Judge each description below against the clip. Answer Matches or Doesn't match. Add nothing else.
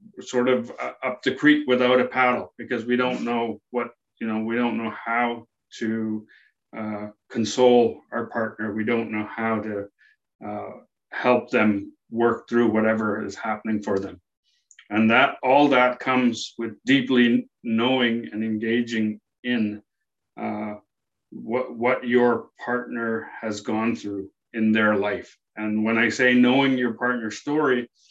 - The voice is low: Matches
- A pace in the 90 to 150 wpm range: Matches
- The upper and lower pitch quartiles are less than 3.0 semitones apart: Matches